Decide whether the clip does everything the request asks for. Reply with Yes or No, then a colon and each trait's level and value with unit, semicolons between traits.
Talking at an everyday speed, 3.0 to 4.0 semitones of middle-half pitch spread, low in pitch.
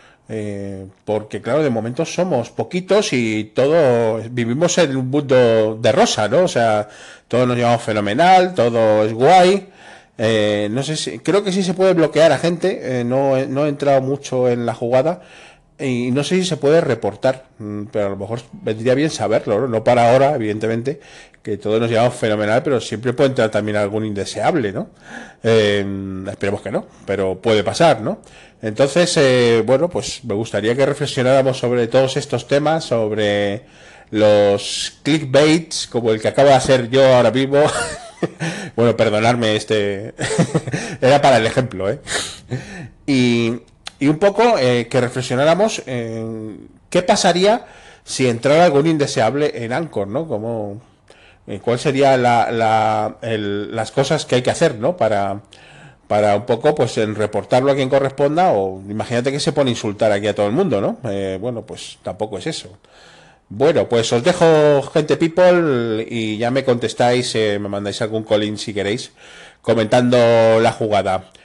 No: average, 165 wpm; average, 4.6 semitones; low, 120 Hz